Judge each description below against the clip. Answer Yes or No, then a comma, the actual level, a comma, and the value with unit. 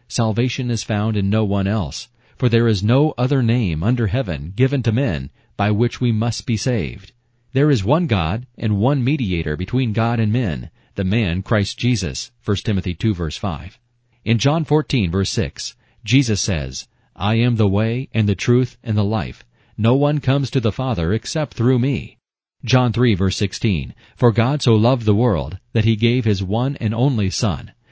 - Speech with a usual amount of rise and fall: Yes, average, 3.5 semitones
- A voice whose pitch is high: No, low, 115 Hz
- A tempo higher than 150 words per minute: Yes, average, 185 wpm